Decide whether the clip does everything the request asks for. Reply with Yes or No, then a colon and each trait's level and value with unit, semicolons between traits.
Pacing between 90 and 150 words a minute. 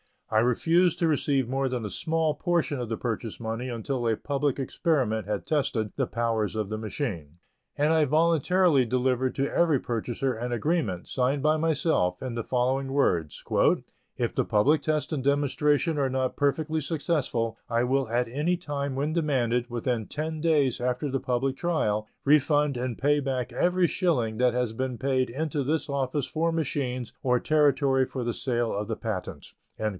No: average, 175 wpm